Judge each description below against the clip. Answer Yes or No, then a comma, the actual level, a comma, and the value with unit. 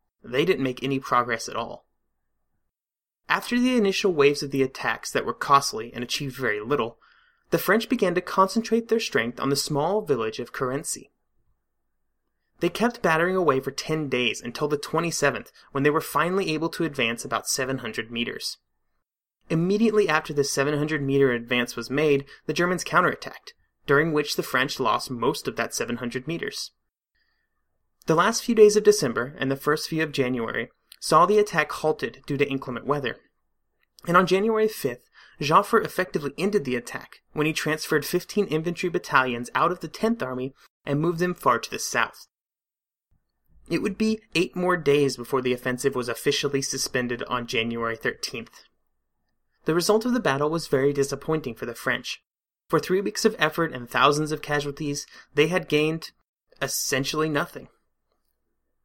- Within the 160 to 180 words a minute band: Yes, average, 170 wpm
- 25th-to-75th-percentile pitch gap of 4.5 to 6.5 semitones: Yes, average, 5.3 semitones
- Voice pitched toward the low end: No, medium, 150 Hz